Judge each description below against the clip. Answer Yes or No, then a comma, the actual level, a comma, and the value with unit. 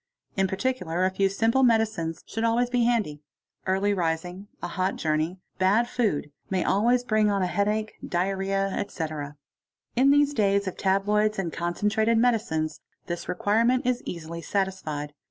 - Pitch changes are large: No, average, 4.3 semitones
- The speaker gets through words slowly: No, average, 150 wpm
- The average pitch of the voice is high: Yes, high, 195 Hz